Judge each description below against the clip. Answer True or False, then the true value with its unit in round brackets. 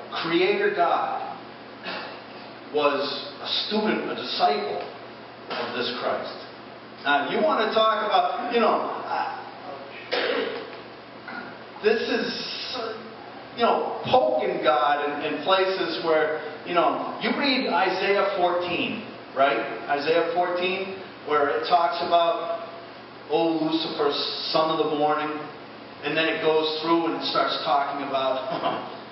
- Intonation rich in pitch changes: True (5.9 semitones)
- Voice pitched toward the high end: False (165 Hz)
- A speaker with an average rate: False (120 wpm)